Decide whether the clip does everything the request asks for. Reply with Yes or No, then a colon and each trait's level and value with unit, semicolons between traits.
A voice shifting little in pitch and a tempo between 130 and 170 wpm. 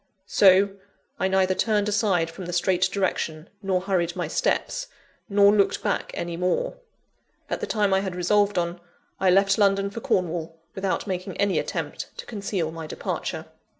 Yes: narrow, 2.2 semitones; average, 165 wpm